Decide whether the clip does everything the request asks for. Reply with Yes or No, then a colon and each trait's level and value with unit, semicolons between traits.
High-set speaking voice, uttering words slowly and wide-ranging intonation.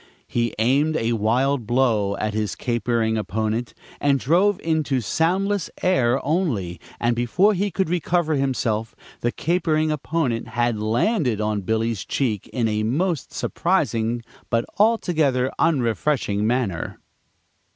No: low, 125 Hz; slow, 125 wpm; wide, 6.1 semitones